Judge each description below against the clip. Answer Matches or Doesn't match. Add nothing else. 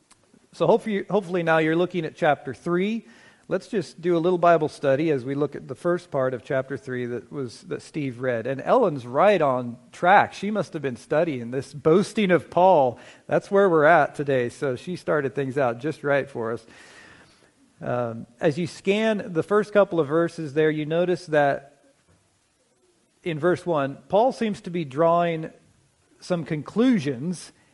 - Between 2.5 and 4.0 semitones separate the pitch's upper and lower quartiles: Doesn't match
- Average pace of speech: Matches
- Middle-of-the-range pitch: Matches